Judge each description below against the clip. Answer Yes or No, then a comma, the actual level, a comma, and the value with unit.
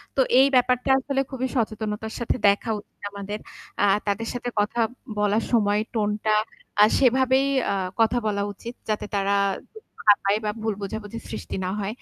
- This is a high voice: Yes, high, 220 Hz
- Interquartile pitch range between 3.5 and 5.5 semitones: No, average, 3.1 semitones